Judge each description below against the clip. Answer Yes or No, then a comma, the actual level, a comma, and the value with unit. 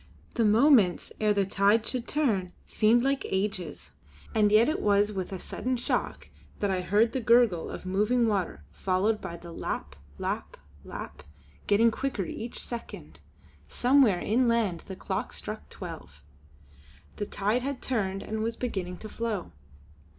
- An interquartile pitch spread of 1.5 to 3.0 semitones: No, average, 3.6 semitones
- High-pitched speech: Yes, high, 210 Hz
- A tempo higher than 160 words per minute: No, average, 150 wpm